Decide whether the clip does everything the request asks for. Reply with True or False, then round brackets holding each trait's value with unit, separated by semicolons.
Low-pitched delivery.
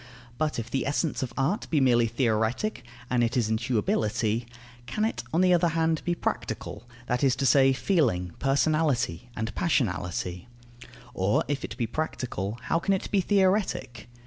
True (130 Hz)